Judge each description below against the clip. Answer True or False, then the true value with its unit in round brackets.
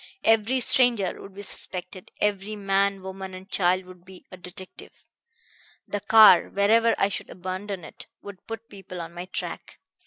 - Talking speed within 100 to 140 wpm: False (160 wpm)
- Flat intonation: True (1.9 semitones)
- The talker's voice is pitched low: False (195 Hz)